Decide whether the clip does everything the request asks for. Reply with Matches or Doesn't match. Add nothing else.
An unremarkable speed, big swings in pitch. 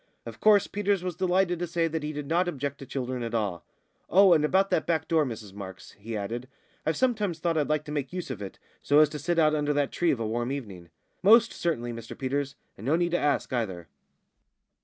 Doesn't match